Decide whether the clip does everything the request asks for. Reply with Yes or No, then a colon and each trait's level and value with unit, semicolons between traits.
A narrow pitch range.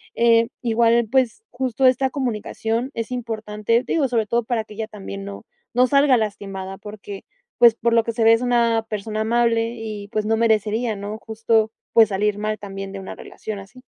Yes: narrow, 2.0 semitones